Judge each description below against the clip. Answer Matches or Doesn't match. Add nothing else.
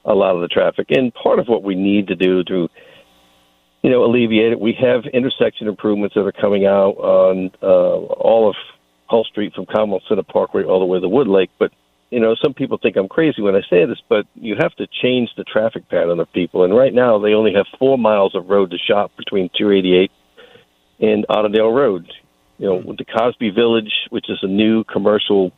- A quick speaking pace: Matches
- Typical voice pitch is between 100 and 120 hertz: Matches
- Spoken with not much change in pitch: Doesn't match